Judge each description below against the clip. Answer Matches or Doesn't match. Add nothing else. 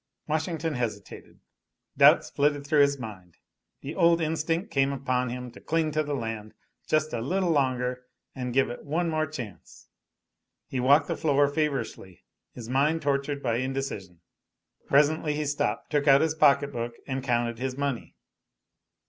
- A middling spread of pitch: Matches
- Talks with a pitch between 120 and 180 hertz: Matches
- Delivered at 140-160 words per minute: Matches